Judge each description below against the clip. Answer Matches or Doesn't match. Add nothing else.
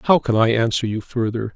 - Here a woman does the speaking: Doesn't match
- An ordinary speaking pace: Doesn't match